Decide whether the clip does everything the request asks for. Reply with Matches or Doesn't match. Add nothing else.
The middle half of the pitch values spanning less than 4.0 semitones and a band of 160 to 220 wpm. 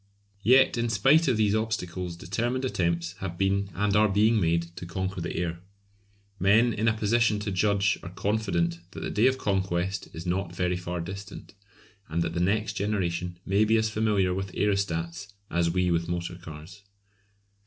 Matches